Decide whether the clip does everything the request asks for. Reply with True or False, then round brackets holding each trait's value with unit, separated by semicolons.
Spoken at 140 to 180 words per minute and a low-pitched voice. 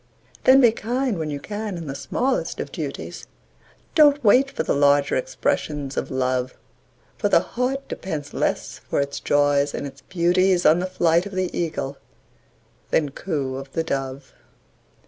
False (165 wpm; 160 Hz)